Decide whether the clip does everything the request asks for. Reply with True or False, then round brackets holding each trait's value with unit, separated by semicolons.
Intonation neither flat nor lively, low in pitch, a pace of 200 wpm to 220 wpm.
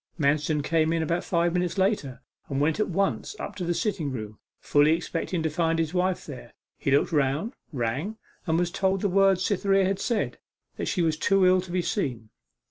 False (4.2 semitones; 170 Hz; 205 wpm)